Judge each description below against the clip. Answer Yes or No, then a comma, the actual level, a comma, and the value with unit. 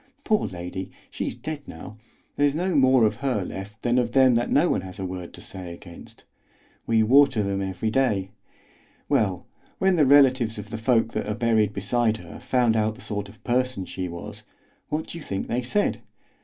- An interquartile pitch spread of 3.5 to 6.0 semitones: Yes, average, 4.9 semitones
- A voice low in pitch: Yes, low, 115 Hz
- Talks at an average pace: Yes, average, 195 wpm